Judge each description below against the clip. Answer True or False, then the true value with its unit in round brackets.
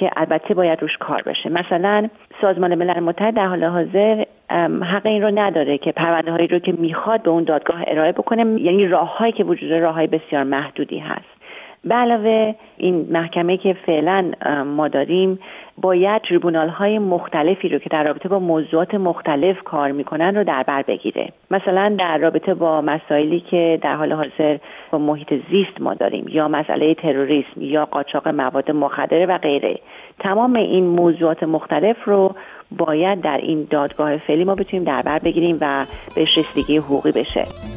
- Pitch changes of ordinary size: True (3.9 semitones)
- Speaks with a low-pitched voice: False (165 Hz)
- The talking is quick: True (165 wpm)